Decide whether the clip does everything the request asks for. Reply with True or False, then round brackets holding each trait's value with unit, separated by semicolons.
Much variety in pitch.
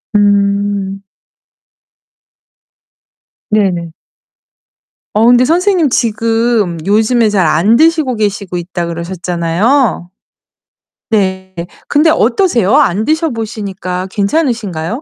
False (4.5 semitones)